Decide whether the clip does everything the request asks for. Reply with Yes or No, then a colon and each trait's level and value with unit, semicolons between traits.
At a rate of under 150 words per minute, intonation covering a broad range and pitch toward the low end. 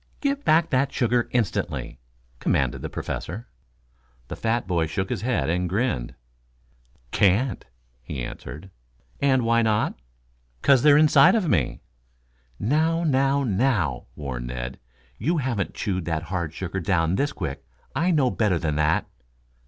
Yes: average, 140 wpm; wide, 8.6 semitones; low, 105 Hz